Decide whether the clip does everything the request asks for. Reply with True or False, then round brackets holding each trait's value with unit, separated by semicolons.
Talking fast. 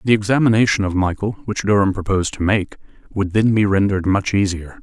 False (175 wpm)